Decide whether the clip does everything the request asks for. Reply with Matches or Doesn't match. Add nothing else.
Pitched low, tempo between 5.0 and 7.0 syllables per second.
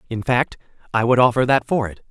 Matches